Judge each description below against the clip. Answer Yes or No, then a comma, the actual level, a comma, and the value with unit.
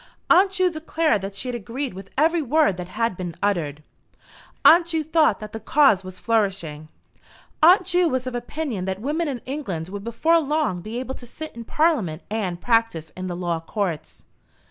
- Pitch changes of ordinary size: No, wide, 8.8 semitones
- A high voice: Yes, high, 230 Hz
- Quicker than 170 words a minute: Yes, average, 190 wpm